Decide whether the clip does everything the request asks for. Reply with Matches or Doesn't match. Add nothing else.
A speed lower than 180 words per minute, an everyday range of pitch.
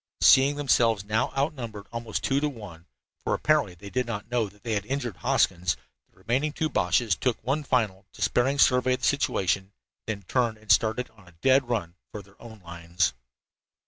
Doesn't match